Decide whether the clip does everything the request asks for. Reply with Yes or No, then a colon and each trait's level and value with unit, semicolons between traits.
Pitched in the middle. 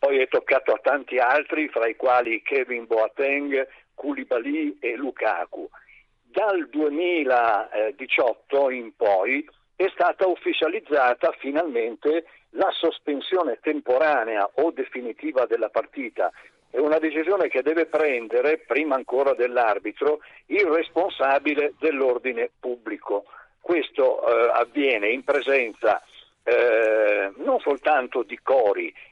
Yes: medium, 170 Hz